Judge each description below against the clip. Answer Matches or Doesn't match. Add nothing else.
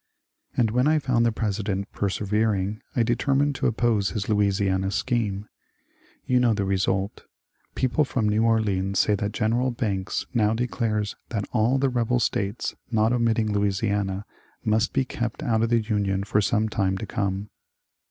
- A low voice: Matches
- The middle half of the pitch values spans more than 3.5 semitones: Doesn't match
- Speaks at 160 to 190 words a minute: Matches